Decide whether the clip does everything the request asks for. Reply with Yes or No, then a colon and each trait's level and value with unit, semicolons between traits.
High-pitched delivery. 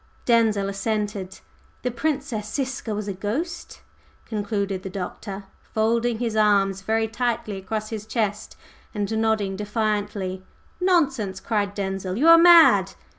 Yes: high, 215 Hz